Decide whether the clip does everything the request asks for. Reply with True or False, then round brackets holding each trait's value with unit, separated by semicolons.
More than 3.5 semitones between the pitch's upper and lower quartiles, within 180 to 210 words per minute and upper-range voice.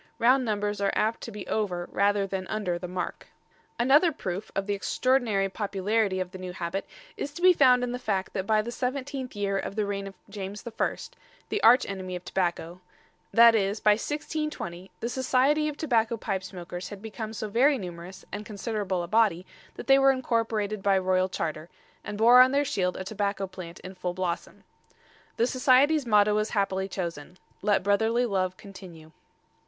True (4.0 semitones; 185 wpm; 205 Hz)